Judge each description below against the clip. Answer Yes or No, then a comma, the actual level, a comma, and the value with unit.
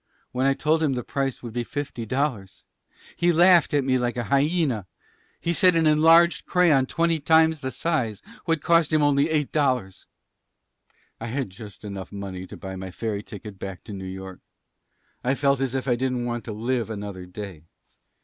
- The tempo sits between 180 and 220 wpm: Yes, average, 190 wpm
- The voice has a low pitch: Yes, low, 130 Hz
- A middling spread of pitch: No, wide, 6.5 semitones